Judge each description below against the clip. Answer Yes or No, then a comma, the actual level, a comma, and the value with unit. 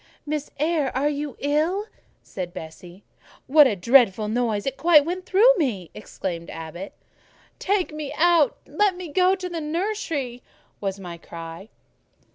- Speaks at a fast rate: No, average, 145 wpm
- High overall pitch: Yes, very high, 285 Hz